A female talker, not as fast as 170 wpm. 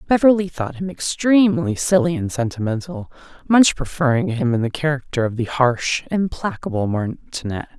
Yes: female; average, 140 wpm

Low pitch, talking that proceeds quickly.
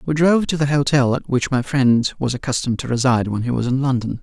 Yes: low, 130 Hz; fast, 255 wpm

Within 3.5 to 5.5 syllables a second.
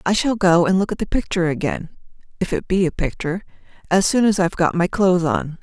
No: 6.4 syllables/s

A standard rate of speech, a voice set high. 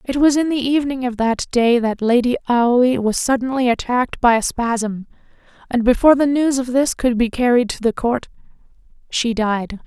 Yes: average, 190 wpm; high, 245 Hz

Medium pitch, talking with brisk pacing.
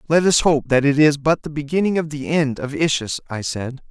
Yes: medium, 145 Hz; fast, 245 wpm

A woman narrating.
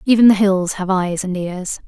Yes: female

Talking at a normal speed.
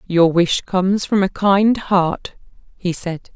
Yes: average, 160 wpm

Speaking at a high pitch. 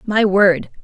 Yes: high, 195 Hz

